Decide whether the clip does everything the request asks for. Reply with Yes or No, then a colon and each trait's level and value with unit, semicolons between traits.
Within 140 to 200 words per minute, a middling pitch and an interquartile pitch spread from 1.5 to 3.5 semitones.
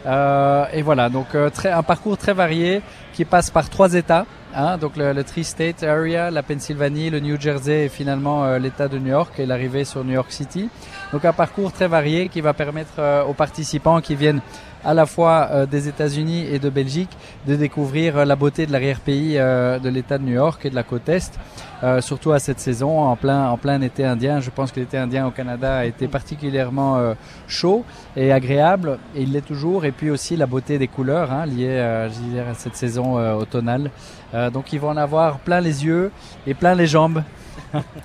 No: average, 215 wpm; medium, 145 Hz; average, 3.1 semitones